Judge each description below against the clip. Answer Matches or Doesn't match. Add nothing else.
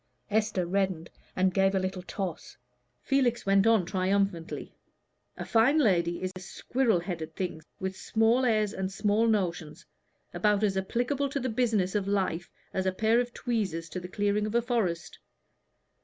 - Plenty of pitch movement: Doesn't match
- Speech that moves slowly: Doesn't match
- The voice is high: Matches